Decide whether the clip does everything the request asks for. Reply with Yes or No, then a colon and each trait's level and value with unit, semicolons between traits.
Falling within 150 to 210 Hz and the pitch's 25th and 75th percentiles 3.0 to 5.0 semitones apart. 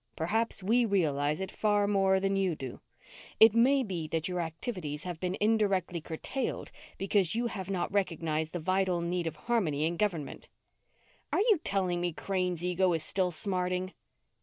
Yes: medium, 185 Hz; average, 3.3 semitones